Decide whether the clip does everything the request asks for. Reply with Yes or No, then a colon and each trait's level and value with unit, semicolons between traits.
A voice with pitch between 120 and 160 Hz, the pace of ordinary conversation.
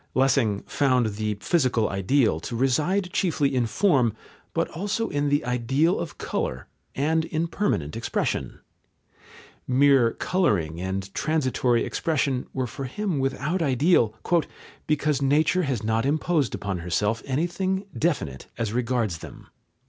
No: low, 135 Hz; slow, 130 wpm